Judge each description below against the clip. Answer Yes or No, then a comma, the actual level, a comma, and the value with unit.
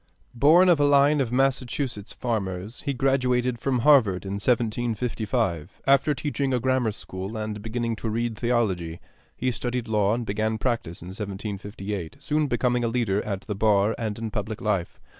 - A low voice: Yes, low, 115 Hz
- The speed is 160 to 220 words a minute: Yes, average, 165 wpm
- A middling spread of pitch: Yes, average, 3.6 semitones